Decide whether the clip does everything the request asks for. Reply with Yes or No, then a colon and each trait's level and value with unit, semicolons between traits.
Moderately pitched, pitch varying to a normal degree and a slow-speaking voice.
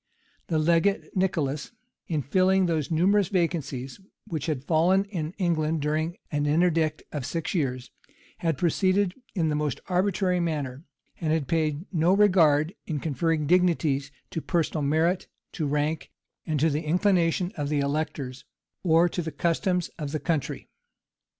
No: medium, 160 Hz; average, 3.1 semitones; average, 145 wpm